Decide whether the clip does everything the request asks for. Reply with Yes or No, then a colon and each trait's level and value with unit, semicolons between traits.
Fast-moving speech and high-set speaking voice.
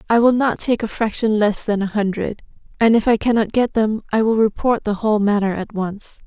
Yes: fast, 230 wpm; high, 215 Hz